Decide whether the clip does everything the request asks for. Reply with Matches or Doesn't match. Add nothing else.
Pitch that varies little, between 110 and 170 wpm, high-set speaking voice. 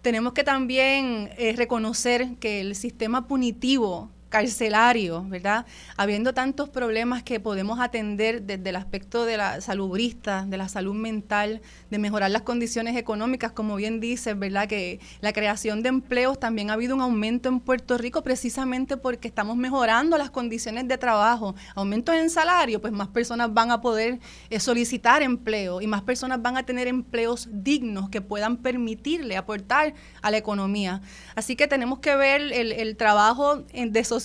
Doesn't match